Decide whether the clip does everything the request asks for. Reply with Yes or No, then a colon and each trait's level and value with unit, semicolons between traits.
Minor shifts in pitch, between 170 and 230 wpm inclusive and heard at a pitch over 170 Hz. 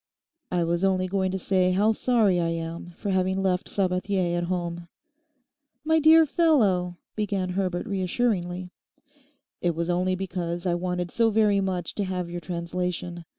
No: narrow, 2.1 semitones; average, 155 wpm; medium, 185 Hz